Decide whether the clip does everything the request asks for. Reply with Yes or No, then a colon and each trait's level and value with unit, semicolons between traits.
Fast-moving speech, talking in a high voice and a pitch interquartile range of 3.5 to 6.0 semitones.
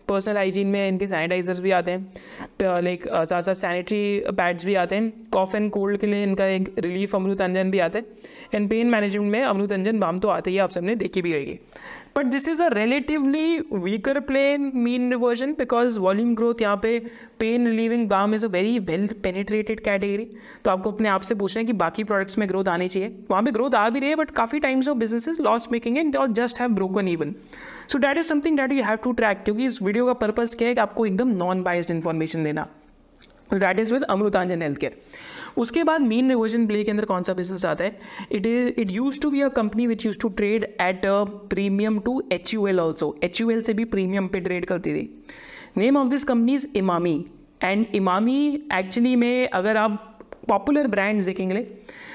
Yes: fast, 220 wpm; high, 215 Hz; average, 3.9 semitones